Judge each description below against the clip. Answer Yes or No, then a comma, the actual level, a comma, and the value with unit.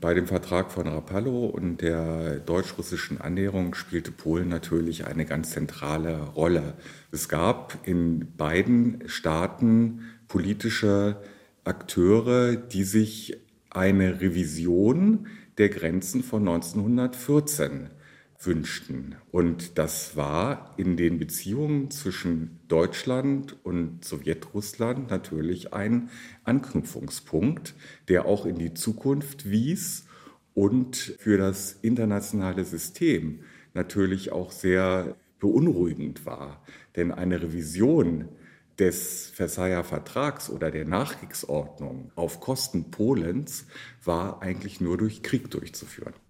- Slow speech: Yes, slow, 100 wpm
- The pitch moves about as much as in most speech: Yes, average, 4.6 semitones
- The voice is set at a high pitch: No, very low, 95 Hz